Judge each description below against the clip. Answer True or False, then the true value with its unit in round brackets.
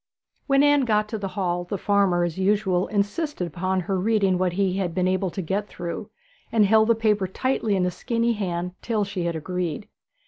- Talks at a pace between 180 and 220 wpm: True (205 wpm)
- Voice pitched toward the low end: False (195 Hz)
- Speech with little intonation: False (3.0 semitones)